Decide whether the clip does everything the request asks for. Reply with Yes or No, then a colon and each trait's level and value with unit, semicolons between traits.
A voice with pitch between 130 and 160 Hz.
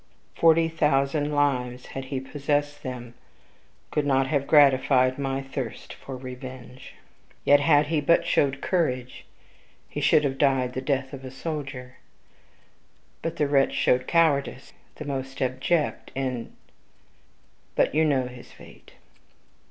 Yes: low, 135 Hz